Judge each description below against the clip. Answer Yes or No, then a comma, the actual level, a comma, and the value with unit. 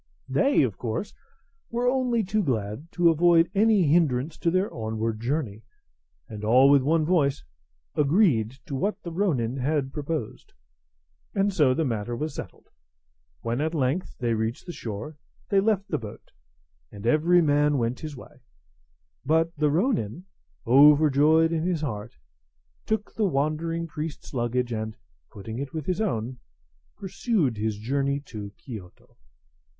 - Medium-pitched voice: Yes, medium, 145 Hz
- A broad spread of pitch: Yes, wide, 6.2 semitones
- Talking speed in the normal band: Yes, average, 145 wpm